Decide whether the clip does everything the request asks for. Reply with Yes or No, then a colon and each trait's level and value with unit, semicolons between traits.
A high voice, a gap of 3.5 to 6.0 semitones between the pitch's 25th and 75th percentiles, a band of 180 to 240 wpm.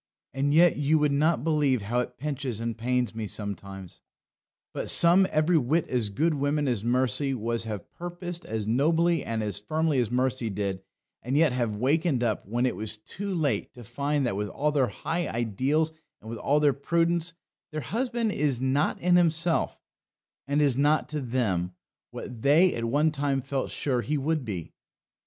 No: low, 135 Hz; average, 5.0 semitones; average, 185 wpm